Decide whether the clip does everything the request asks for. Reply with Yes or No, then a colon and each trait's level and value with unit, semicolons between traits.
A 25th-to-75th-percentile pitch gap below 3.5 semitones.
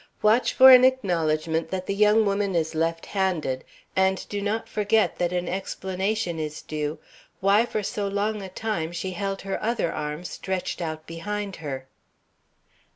No: average, 4.0 semitones